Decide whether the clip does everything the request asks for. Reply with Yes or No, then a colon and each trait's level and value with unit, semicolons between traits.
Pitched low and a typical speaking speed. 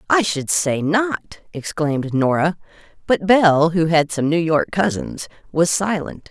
No: medium, 165 Hz; average, 150 wpm